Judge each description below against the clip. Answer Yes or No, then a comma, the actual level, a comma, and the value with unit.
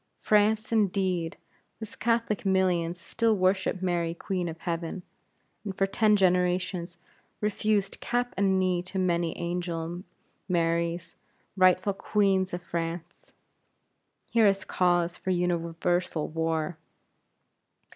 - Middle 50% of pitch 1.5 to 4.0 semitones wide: Yes, narrow, 2.4 semitones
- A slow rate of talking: Yes, slow, 110 wpm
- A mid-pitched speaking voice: Yes, medium, 180 Hz